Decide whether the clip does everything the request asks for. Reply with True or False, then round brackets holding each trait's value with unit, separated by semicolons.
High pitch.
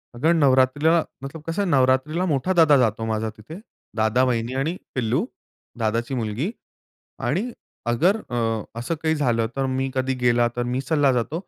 False (130 Hz)